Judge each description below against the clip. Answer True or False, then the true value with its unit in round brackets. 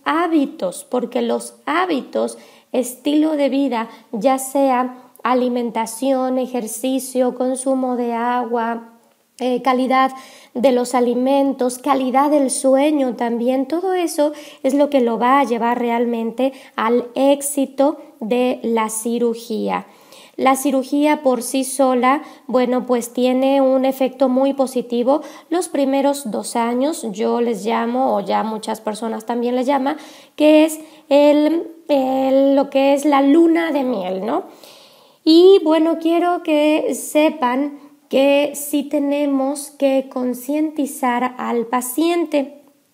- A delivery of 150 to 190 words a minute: False (125 wpm)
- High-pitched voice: True (265 Hz)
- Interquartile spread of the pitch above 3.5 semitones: False (2.6 semitones)